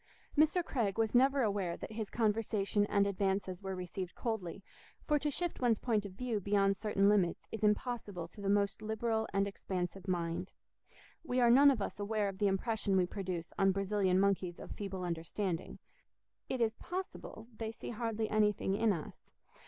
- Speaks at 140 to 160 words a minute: No, average, 175 wpm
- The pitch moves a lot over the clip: No, average, 2.8 semitones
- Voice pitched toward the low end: No, high, 205 Hz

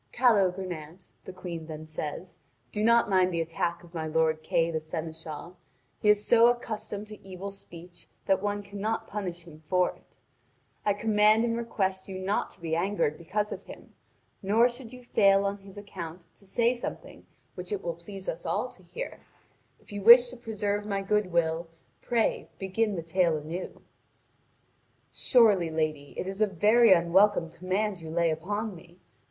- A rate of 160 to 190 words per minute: Yes, average, 175 wpm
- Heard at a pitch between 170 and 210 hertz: Yes, high, 190 Hz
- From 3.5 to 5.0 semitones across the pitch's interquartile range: Yes, average, 3.8 semitones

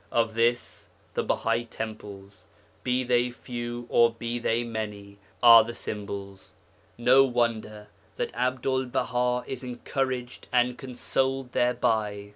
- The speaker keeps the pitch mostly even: Yes, narrow, 2.1 semitones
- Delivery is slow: Yes, slow, 120 wpm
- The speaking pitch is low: Yes, low, 120 Hz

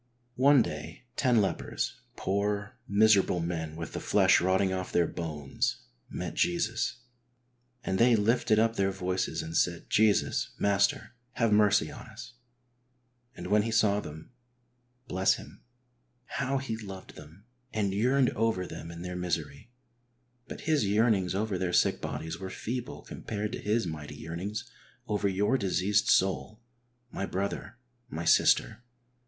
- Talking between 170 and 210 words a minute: No, average, 150 wpm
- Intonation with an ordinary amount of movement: Yes, average, 4.0 semitones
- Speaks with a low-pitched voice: Yes, low, 100 Hz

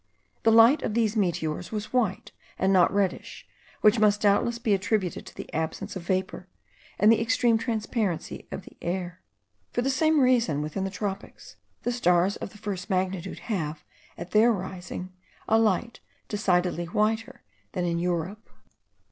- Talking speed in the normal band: Yes, average, 160 wpm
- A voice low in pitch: No, high, 200 Hz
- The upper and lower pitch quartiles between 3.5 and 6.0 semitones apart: Yes, average, 3.9 semitones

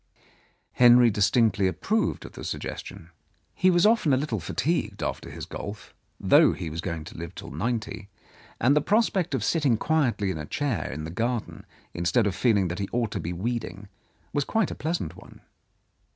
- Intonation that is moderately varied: No, wide, 7.4 semitones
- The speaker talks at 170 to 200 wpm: Yes, average, 190 wpm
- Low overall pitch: Yes, low, 115 Hz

